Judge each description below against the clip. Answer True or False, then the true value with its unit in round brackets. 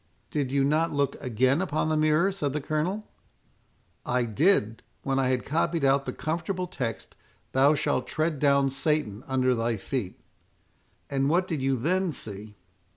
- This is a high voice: False (140 Hz)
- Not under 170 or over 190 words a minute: False (160 wpm)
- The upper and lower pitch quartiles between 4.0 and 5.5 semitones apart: False (3.4 semitones)